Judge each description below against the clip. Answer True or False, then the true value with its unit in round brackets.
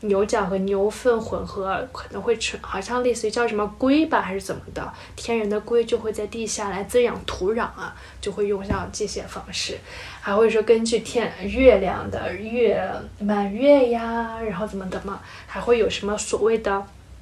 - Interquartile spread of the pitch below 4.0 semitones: True (2.8 semitones)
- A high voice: True (220 Hz)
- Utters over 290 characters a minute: False (265 characters per minute)